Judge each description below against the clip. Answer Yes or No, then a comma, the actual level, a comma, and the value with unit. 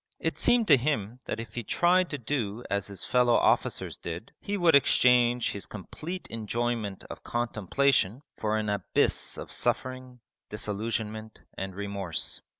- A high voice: No, low, 115 Hz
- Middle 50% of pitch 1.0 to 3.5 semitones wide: No, average, 3.9 semitones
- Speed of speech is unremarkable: Yes, average, 150 wpm